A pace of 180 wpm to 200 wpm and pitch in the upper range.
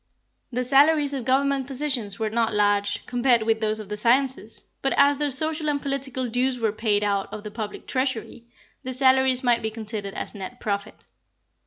Yes: average, 185 wpm; high, 245 Hz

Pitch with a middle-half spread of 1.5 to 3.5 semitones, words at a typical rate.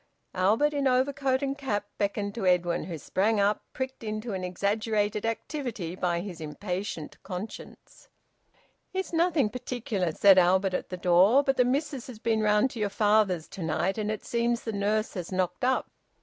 No: average, 5.0 semitones; average, 175 wpm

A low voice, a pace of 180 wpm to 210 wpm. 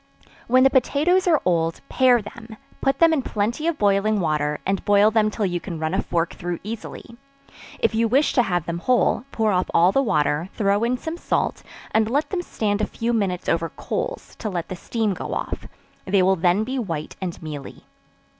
No: high, 210 Hz; fast, 205 wpm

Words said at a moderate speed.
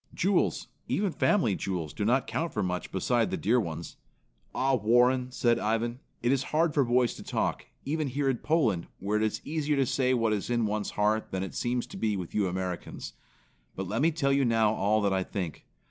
No: fast, 215 wpm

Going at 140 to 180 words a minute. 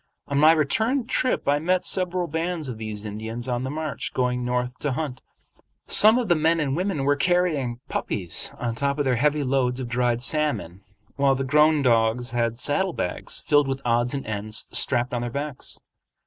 No: average, 190 wpm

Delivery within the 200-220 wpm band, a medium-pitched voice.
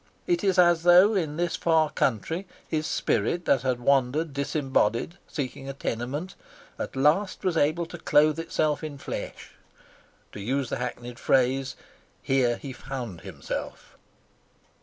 No: average, 140 wpm; medium, 145 Hz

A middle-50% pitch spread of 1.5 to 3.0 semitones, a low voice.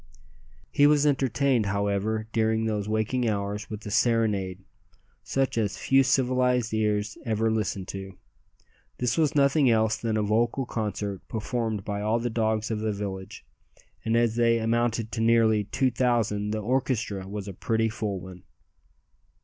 Yes: narrow, 2.4 semitones; low, 110 Hz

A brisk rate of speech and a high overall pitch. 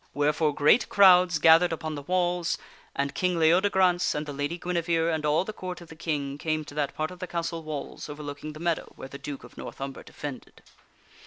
No: fast, 215 wpm; medium, 160 Hz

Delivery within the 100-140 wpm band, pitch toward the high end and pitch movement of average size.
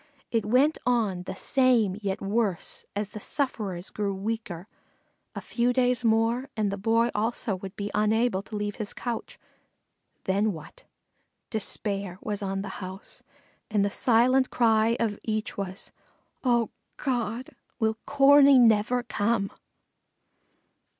Yes: slow, 135 wpm; high, 220 Hz; average, 3.2 semitones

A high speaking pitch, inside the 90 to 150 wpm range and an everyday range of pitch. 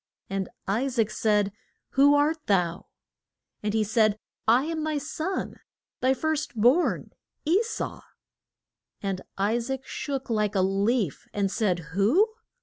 No: high, 230 Hz; average, 140 wpm; wide, 6.2 semitones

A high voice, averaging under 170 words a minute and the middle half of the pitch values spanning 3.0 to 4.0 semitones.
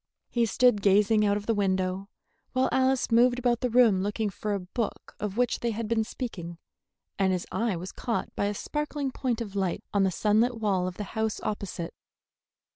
No: high, 210 Hz; average, 200 wpm; average, 3.6 semitones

